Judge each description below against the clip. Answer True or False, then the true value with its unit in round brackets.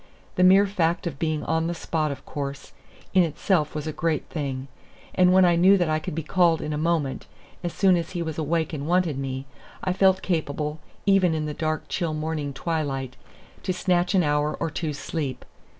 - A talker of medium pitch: True (160 Hz)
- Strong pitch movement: False (2.9 semitones)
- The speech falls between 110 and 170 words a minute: False (205 wpm)